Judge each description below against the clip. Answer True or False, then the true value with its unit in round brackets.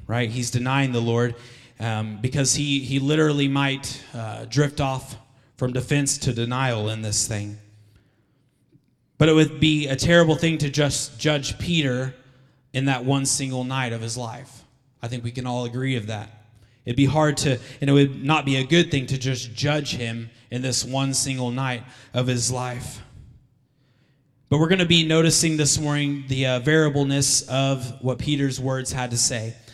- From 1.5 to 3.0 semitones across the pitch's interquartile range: True (2.6 semitones)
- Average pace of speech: True (180 wpm)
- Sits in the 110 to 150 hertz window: True (130 Hz)